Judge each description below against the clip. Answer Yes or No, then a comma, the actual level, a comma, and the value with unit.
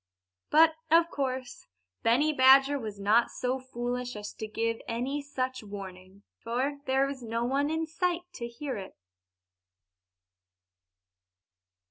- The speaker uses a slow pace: Yes, slow, 120 wpm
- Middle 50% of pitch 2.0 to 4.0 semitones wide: Yes, average, 3.7 semitones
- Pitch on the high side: Yes, very high, 255 Hz